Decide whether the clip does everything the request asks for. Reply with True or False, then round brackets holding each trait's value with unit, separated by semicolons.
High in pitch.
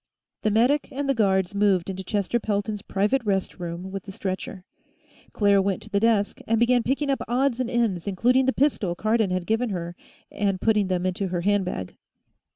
True (205 Hz)